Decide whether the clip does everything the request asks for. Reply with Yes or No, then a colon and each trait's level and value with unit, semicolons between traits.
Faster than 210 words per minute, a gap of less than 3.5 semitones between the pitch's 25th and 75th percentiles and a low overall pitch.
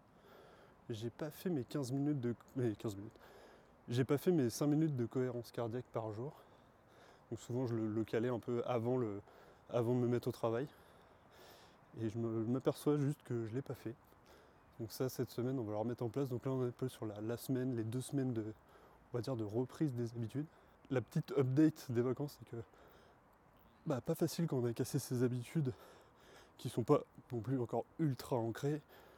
Yes: fast, 220 wpm; average, 3.0 semitones; low, 125 Hz